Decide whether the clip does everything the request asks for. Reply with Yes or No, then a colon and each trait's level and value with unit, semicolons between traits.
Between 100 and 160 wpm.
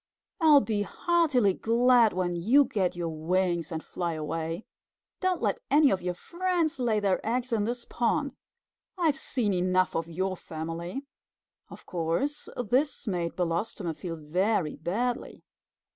Yes: average, 145 wpm